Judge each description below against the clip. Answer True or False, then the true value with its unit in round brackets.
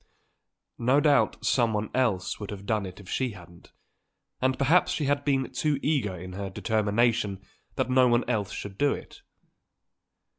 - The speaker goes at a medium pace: True (160 wpm)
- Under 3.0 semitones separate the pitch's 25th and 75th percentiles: False (4.9 semitones)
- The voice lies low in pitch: True (115 Hz)